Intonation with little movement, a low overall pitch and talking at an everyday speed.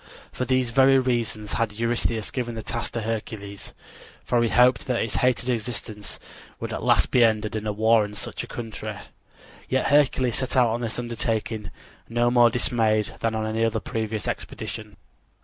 Yes: narrow, 2.0 semitones; low, 115 Hz; average, 175 wpm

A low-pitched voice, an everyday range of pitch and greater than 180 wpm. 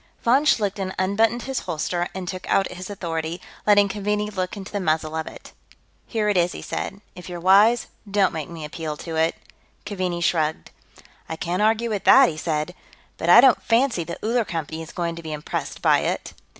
No: medium, 185 Hz; average, 4.2 semitones; average, 200 wpm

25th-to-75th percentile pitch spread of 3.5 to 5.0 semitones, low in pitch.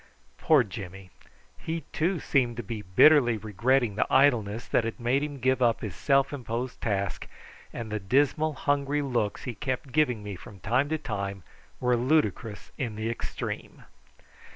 Yes: average, 4.7 semitones; low, 120 Hz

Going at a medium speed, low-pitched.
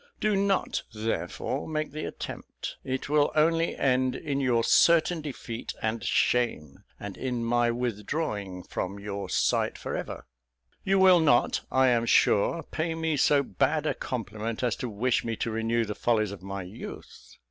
Yes: average, 165 wpm; low, 125 Hz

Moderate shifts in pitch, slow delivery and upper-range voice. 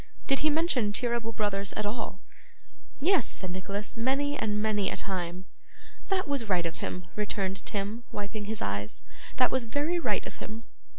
No: average, 4.7 semitones; average, 170 wpm; high, 215 Hz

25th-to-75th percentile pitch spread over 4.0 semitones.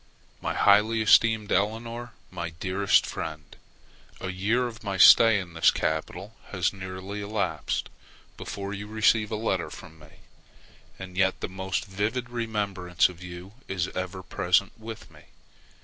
No: average, 3.0 semitones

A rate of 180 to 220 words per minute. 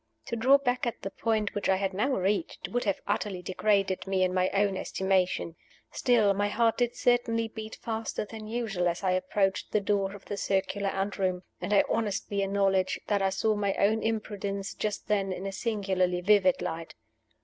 Yes: average, 190 wpm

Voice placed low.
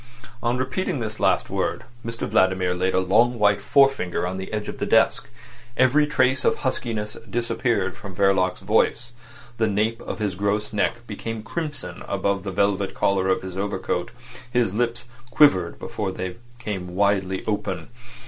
Yes: low, 105 Hz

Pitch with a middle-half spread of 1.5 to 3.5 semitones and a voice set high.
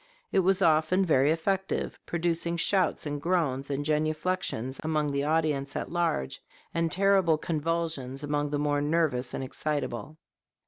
No: average, 2.8 semitones; medium, 155 Hz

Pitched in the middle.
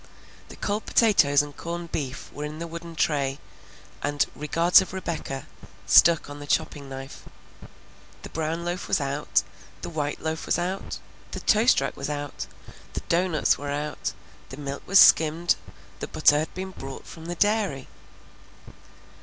Yes: medium, 155 Hz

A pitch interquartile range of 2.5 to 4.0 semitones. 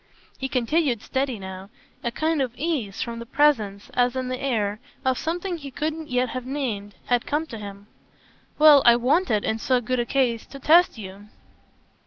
No: average, 4.7 semitones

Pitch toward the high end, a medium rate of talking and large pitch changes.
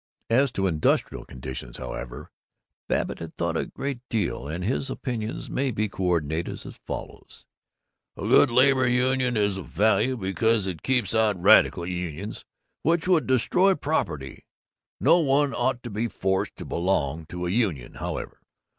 No: low, 105 Hz; average, 155 wpm; wide, 6.8 semitones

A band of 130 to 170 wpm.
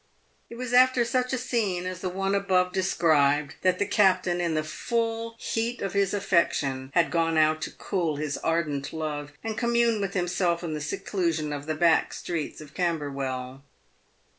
No: average, 180 wpm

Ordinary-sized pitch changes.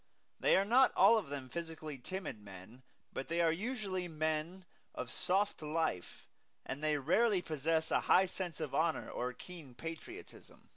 Yes: average, 4.4 semitones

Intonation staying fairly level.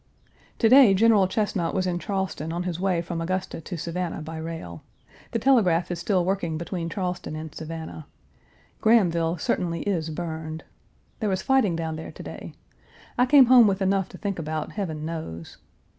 No: average, 3.4 semitones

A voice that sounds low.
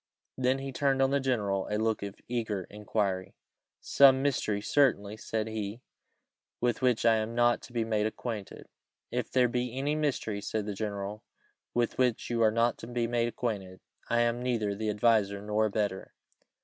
Yes: low, 115 Hz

